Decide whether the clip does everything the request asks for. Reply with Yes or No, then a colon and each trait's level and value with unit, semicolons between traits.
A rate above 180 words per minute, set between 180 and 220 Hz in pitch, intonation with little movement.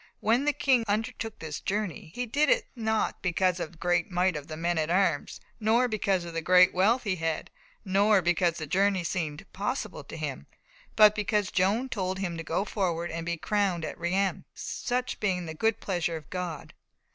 No: average, 195 wpm; medium, 185 Hz; average, 3.8 semitones